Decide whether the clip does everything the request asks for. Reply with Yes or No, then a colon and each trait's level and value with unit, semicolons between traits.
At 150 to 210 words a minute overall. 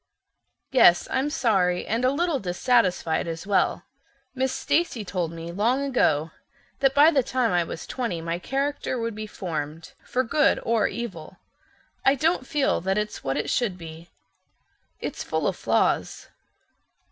Yes: average, 155 wpm